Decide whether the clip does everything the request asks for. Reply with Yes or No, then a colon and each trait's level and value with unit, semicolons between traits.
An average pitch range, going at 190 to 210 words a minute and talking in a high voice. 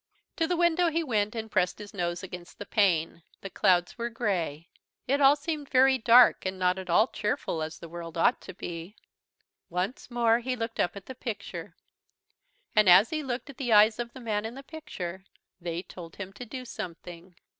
No: wide, 5.8 semitones; average, 200 wpm; high, 210 Hz